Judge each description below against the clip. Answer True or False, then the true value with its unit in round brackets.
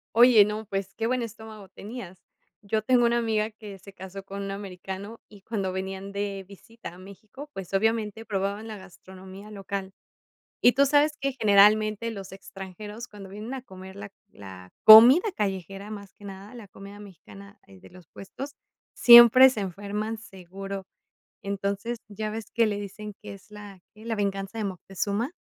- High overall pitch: True (205 Hz)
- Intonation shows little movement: True (2.3 semitones)